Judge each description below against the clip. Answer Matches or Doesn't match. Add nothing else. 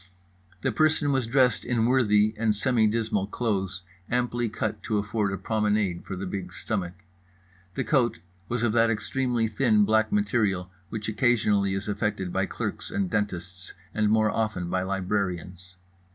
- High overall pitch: Doesn't match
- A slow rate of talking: Doesn't match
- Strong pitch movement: Doesn't match